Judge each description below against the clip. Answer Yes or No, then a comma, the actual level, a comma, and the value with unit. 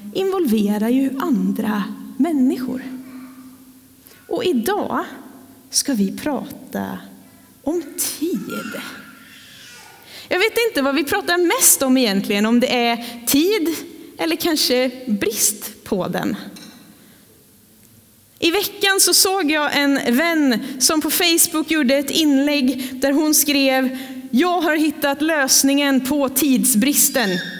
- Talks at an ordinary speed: No, slow, 110 wpm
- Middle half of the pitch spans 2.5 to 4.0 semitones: Yes, average, 3.7 semitones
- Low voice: No, very high, 275 Hz